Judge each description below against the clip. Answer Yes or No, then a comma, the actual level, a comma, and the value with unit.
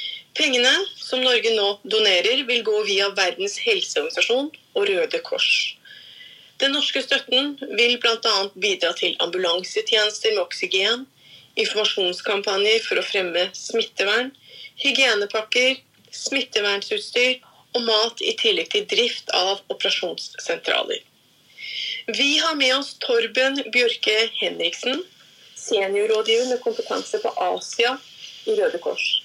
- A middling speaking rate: No, slow, 110 wpm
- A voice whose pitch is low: No, very high, 270 Hz